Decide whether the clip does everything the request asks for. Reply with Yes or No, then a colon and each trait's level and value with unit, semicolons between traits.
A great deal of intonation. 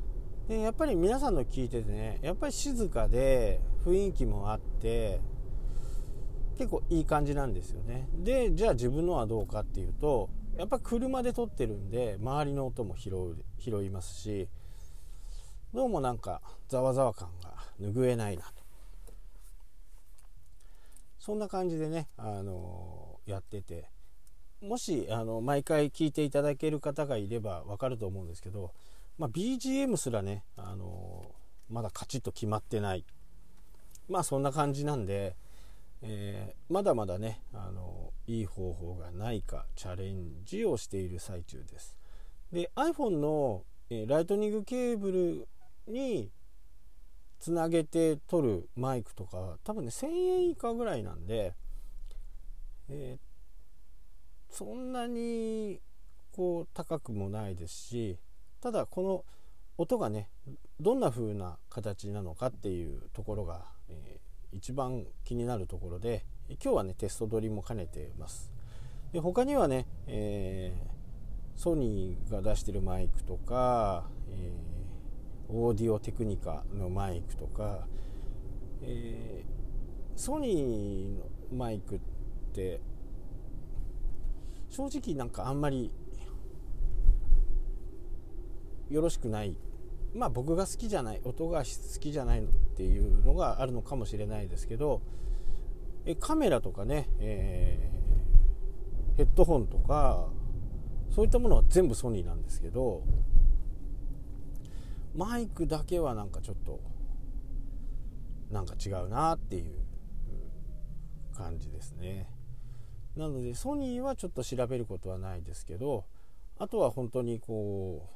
Yes: wide, 6.7 semitones